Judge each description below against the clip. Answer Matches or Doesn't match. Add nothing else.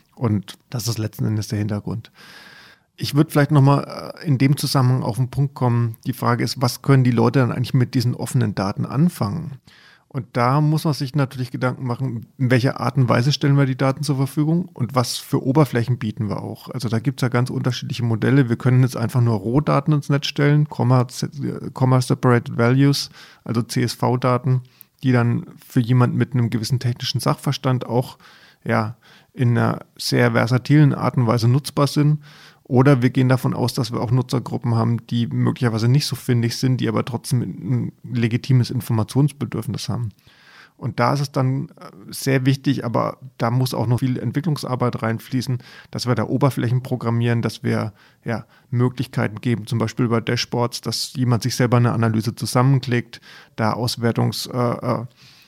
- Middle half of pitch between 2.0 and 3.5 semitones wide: Matches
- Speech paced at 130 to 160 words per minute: Doesn't match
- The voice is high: Doesn't match